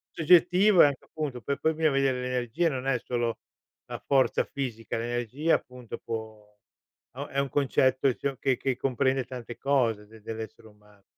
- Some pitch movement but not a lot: Yes, average, 3.3 semitones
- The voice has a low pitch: Yes, low, 130 Hz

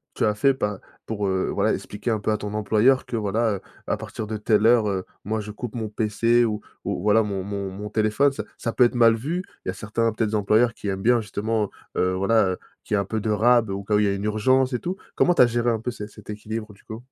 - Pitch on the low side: Yes, low, 110 Hz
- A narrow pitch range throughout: Yes, narrow, 2.0 semitones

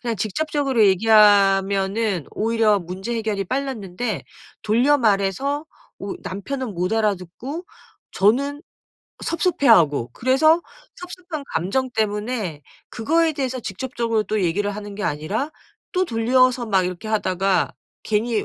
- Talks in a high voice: Yes, high, 220 Hz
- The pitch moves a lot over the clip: No, average, 5.0 semitones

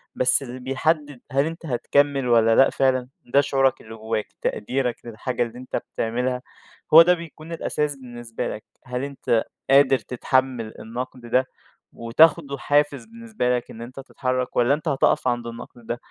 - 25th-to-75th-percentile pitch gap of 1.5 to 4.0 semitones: Yes, average, 2.9 semitones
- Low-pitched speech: Yes, low, 130 Hz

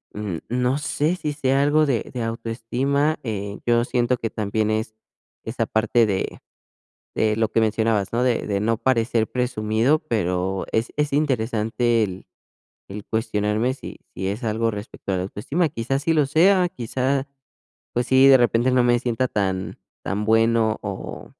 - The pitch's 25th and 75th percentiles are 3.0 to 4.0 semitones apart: Yes, average, 3.4 semitones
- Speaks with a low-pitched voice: Yes, low, 115 Hz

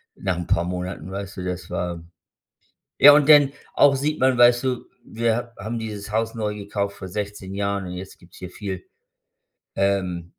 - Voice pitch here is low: Yes, low, 100 Hz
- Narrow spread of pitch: No, average, 4.2 semitones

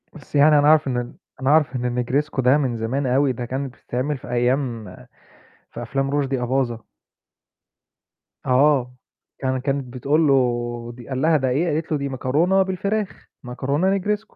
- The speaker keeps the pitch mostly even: No, average, 3.2 semitones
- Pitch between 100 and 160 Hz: Yes, low, 135 Hz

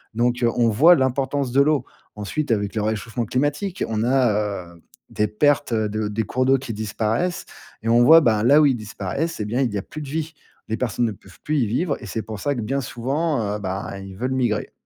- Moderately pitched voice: No, low, 120 Hz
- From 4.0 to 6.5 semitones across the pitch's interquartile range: Yes, average, 4.6 semitones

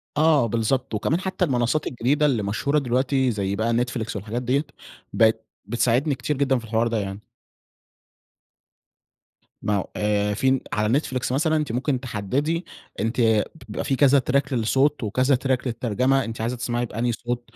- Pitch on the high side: No, low, 125 Hz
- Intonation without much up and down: No, average, 3.5 semitones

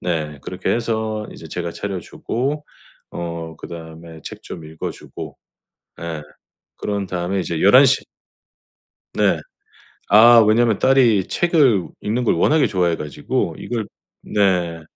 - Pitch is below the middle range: Yes, very low, 95 Hz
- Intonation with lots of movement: Yes, wide, 5.7 semitones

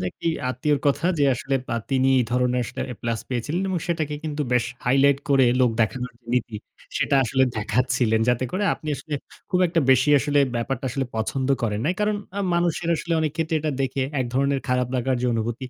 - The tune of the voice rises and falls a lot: No, average, 3.4 semitones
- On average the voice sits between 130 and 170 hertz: Yes, low, 135 Hz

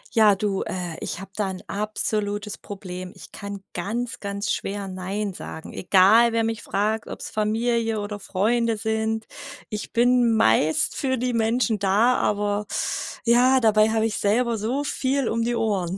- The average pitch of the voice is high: Yes, high, 215 Hz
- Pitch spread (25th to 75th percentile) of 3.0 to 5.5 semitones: No, narrow, 2.5 semitones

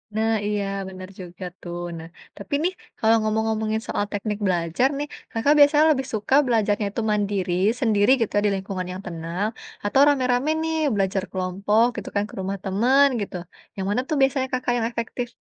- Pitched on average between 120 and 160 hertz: No, high, 210 Hz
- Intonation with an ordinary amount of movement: Yes, average, 4.2 semitones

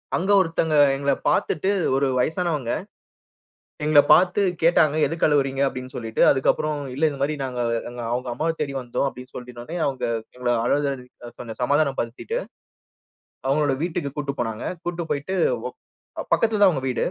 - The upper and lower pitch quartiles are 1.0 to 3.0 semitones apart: No, average, 4.1 semitones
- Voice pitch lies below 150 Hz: Yes, medium, 140 Hz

